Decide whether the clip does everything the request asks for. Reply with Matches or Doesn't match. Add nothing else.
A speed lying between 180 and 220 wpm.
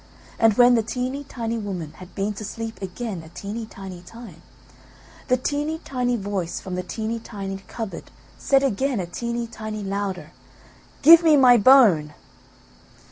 Doesn't match